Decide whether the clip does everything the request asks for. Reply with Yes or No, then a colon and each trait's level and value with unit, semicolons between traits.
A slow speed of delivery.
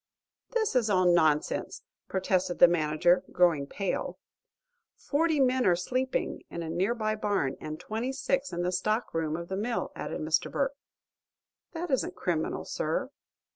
No: average, 155 wpm